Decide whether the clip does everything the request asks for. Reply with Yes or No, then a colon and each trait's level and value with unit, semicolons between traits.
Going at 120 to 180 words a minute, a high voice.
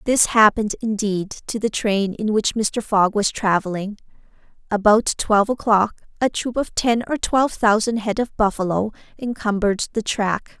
Yes: average, 160 wpm; high, 215 Hz